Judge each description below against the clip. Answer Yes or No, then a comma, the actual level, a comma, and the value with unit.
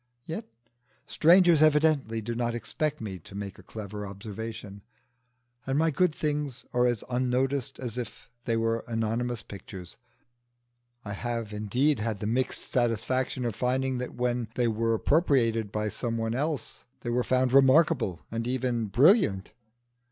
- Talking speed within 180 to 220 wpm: No, average, 150 wpm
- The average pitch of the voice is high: No, low, 120 Hz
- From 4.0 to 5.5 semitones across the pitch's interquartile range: No, average, 3.2 semitones